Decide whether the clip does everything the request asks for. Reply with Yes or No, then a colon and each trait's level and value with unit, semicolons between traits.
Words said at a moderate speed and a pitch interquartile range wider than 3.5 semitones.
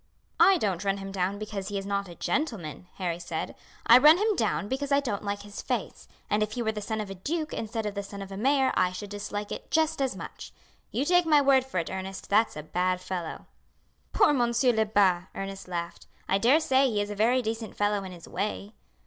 No: fast, 230 wpm; average, 4.6 semitones